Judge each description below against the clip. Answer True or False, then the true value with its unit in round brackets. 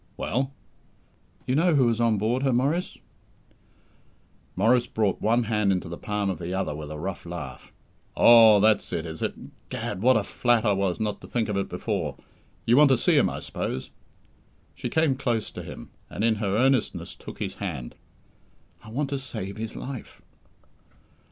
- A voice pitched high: False (110 Hz)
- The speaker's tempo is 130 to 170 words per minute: False (185 wpm)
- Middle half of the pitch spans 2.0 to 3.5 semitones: False (4.3 semitones)